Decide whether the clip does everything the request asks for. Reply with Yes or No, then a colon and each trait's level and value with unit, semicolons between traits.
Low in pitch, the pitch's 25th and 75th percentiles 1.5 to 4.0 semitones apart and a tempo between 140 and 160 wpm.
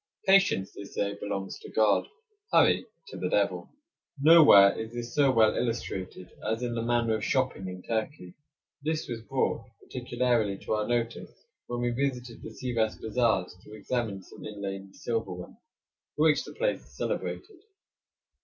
Yes: low, 115 Hz; average, 3.7 semitones; average, 155 wpm